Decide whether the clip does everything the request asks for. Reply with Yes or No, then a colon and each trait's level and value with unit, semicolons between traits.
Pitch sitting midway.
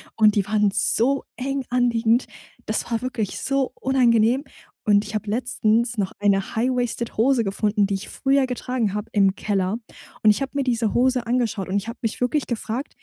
No: high, 230 Hz